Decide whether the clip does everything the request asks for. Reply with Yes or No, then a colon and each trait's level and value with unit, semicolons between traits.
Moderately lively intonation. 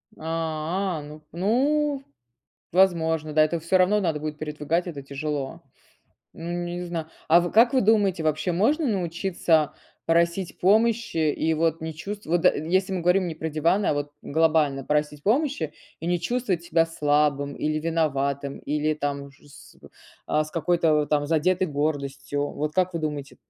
Yes: average, 3.3 semitones